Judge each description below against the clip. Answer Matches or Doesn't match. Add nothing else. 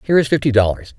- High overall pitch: Doesn't match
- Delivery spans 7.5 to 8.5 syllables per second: Matches